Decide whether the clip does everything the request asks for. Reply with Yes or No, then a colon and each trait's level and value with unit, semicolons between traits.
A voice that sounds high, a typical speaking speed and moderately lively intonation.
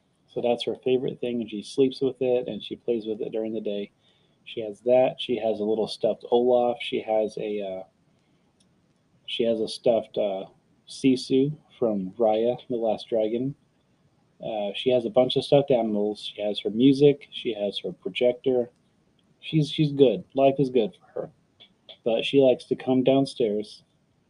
No: low, 125 Hz; average, 180 wpm; average, 3.5 semitones